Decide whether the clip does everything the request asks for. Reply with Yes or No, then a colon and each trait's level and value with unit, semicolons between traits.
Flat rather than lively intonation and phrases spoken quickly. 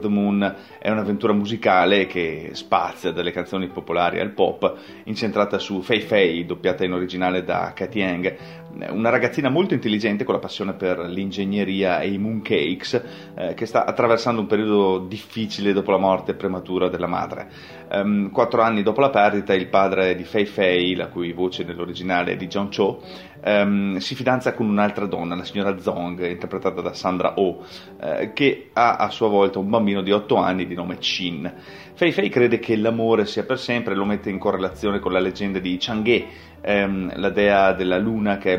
Yes: narrow, 2.1 semitones; fast, 180 wpm